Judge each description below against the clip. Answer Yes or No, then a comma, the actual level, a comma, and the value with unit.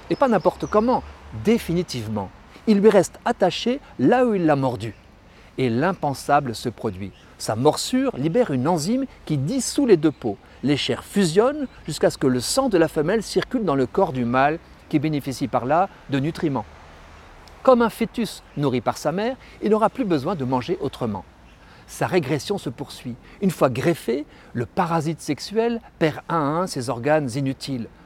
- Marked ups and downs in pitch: Yes, wide, 8.0 semitones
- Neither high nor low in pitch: Yes, medium, 150 Hz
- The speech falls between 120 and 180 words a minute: Yes, average, 175 wpm